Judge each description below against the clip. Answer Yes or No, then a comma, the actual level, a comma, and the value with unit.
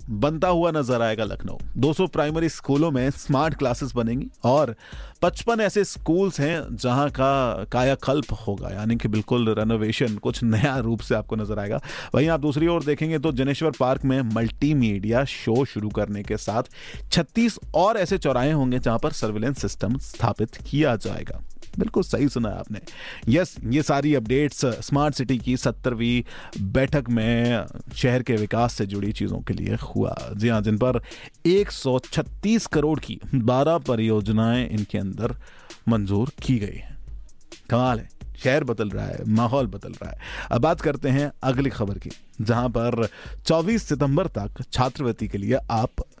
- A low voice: Yes, low, 125 Hz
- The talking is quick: No, average, 155 wpm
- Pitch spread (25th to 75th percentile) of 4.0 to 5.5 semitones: Yes, average, 4.4 semitones